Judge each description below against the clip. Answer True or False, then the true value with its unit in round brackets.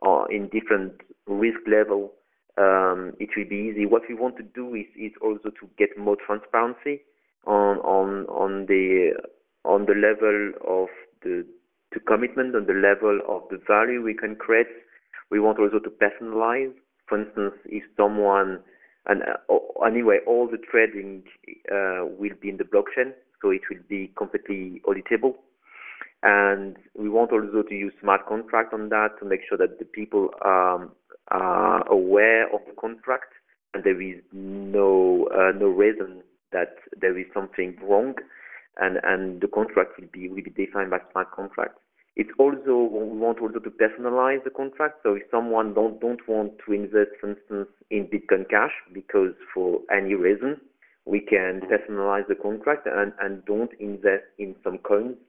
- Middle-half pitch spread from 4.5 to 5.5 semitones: False (3.9 semitones)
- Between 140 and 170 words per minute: True (165 wpm)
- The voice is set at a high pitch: False (105 Hz)